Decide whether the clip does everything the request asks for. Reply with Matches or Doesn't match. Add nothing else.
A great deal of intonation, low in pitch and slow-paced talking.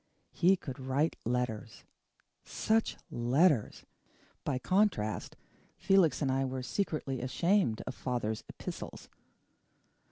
Matches